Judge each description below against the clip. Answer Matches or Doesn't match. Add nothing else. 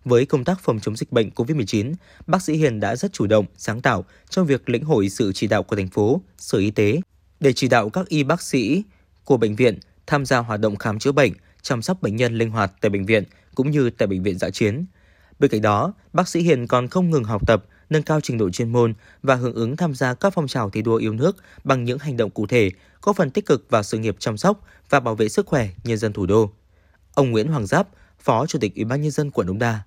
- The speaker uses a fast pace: Matches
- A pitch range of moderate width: Doesn't match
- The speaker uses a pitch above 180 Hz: Doesn't match